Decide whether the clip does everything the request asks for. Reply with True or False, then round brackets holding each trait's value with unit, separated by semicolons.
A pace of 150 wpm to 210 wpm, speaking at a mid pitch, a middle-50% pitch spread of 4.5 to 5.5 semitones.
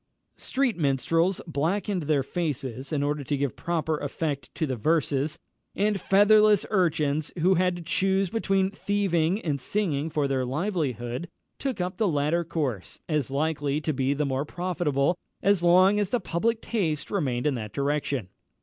True (160 wpm; 160 Hz; 5.0 semitones)